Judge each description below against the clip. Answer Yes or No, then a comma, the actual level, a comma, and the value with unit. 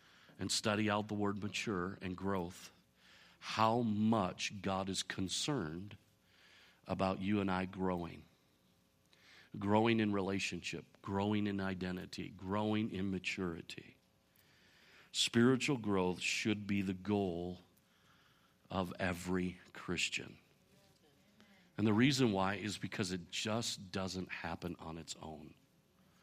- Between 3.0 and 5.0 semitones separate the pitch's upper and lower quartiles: No, narrow, 2.5 semitones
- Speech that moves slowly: Yes, slow, 110 wpm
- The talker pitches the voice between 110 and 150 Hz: No, very low, 95 Hz